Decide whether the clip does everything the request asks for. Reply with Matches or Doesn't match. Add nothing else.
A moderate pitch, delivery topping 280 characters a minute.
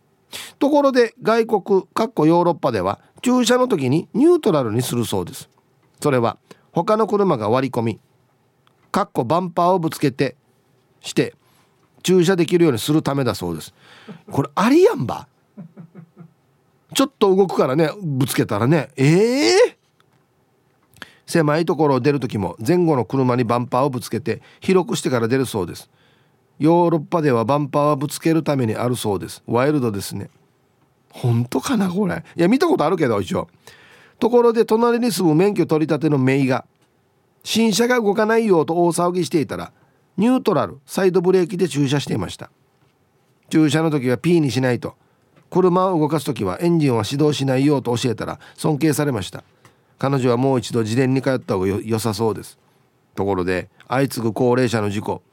Matches